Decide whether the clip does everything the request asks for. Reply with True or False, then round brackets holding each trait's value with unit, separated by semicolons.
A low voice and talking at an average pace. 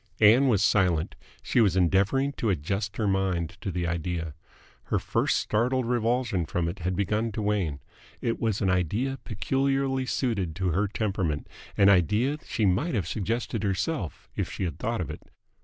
True (100 Hz; 175 wpm)